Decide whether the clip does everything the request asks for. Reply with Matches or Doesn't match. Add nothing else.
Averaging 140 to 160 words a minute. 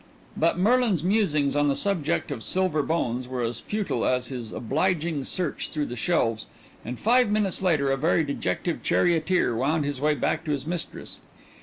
Doesn't match